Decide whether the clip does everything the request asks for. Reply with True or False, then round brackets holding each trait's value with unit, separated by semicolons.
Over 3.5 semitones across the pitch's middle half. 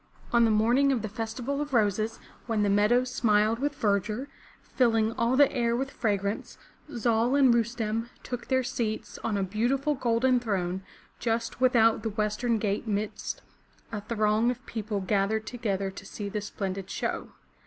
False (2.7 semitones)